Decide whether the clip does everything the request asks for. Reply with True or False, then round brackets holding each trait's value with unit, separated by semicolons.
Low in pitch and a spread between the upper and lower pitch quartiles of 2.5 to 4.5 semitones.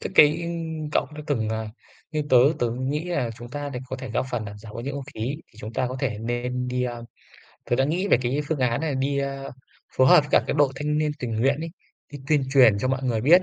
True (130 Hz; 3.5 semitones)